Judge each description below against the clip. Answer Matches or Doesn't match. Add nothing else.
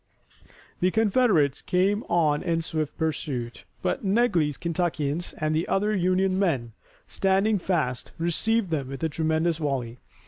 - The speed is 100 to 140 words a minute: Matches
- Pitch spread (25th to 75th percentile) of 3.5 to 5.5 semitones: Matches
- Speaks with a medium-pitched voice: Matches